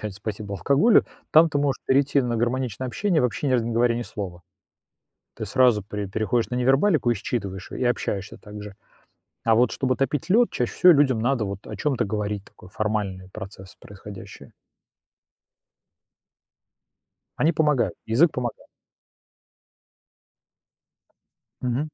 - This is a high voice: No, low, 120 Hz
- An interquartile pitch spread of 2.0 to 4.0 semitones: No, average, 4.7 semitones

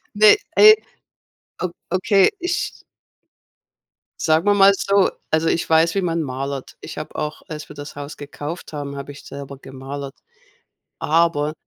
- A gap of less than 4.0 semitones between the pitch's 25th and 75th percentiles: No, average, 4.4 semitones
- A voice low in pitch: No, medium, 155 Hz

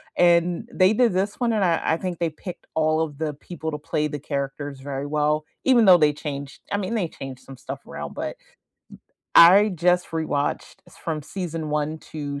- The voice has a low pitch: No, medium, 160 Hz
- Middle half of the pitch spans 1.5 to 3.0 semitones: No, average, 3.6 semitones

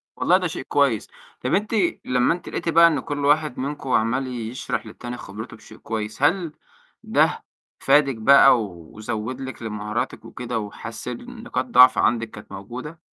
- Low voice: Yes, low, 125 Hz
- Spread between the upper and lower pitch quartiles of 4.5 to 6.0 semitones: Yes, average, 4.8 semitones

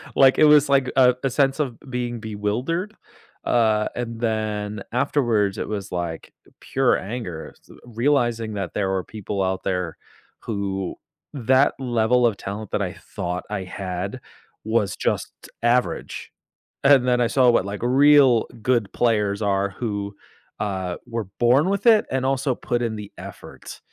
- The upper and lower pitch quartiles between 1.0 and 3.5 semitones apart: No, average, 4.1 semitones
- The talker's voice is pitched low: Yes, low, 115 Hz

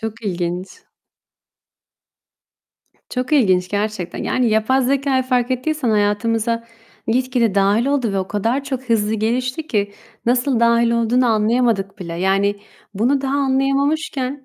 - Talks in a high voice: Yes, high, 235 Hz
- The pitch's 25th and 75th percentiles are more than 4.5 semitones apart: No, average, 4.0 semitones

